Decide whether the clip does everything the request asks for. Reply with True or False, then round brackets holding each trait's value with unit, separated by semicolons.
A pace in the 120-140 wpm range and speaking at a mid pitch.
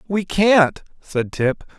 True (135 wpm; 170 Hz)